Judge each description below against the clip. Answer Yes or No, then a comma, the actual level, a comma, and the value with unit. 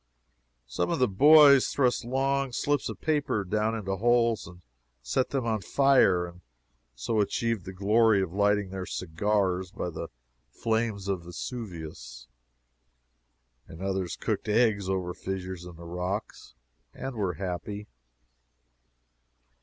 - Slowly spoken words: Yes, slow, 130 wpm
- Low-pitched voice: Yes, low, 100 Hz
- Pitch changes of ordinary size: Yes, average, 4.6 semitones